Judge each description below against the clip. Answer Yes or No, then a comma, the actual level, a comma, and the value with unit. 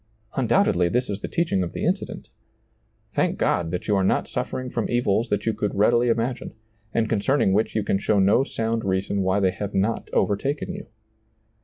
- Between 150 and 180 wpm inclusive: No, average, 190 wpm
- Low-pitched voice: Yes, low, 105 Hz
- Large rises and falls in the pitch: No, average, 3.4 semitones